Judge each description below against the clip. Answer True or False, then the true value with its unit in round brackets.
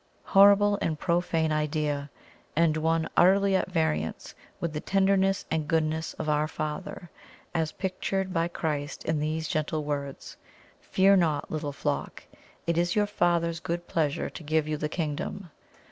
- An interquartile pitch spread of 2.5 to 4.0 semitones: True (3.0 semitones)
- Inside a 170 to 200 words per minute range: False (150 wpm)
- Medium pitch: True (160 Hz)